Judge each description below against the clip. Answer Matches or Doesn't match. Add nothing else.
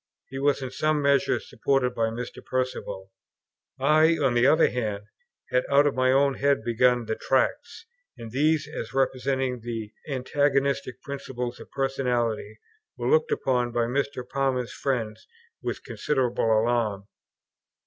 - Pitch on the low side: Matches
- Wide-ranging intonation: Doesn't match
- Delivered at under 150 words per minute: Matches